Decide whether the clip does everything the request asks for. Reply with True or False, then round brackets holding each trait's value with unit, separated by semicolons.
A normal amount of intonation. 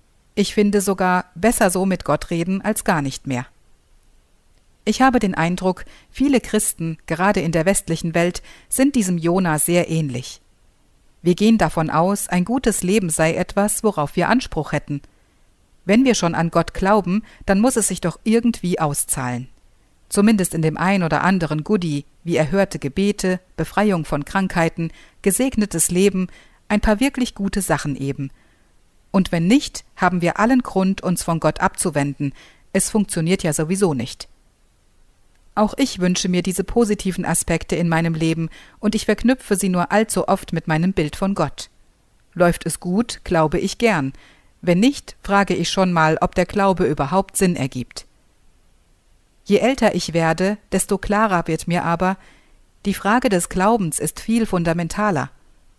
True (3.9 semitones)